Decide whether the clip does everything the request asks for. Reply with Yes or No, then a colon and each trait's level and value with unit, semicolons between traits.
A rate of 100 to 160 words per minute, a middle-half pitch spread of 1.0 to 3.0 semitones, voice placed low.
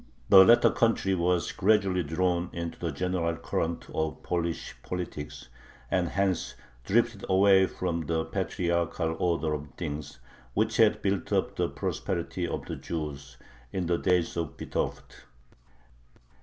Yes: slow, 135 wpm; narrow, 2.5 semitones; very low, 85 Hz